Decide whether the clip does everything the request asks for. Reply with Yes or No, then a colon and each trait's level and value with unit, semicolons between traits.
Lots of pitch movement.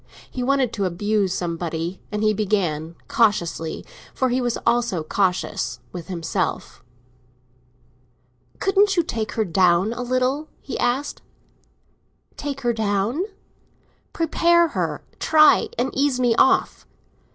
Yes: wide, 6.2 semitones